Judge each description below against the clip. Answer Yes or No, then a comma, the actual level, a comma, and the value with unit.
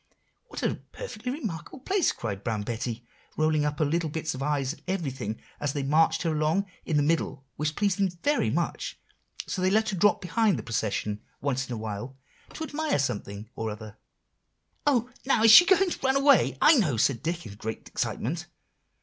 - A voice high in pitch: No, medium, 155 Hz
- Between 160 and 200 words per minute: Yes, average, 195 wpm